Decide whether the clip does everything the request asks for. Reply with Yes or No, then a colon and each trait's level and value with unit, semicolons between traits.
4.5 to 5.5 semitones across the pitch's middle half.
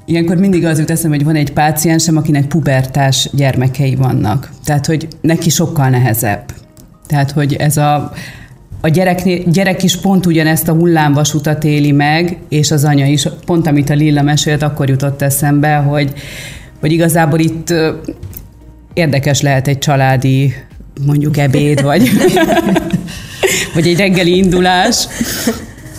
No: average, 2.7 semitones